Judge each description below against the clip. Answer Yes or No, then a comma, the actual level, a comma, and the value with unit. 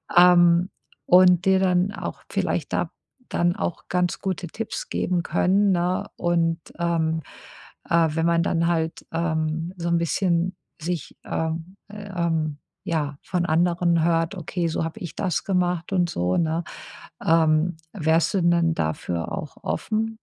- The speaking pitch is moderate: Yes, medium, 170 Hz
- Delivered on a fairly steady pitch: Yes, narrow, 1.7 semitones